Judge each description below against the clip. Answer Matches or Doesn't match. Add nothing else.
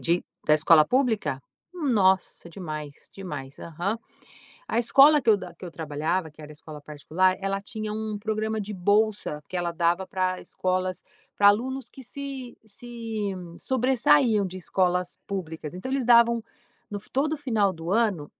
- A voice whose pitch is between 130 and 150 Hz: Doesn't match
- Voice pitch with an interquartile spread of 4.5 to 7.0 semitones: Matches